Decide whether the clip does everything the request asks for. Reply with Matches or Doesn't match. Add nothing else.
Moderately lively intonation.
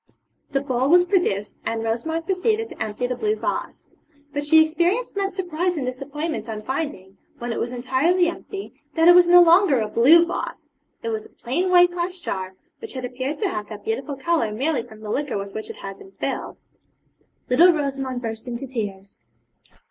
Doesn't match